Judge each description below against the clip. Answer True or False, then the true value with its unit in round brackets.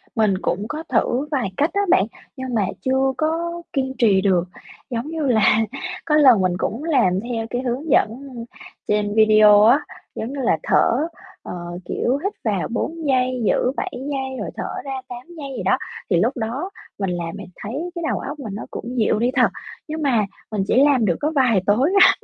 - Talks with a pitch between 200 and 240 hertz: False (250 Hz)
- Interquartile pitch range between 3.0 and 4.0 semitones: False (4.7 semitones)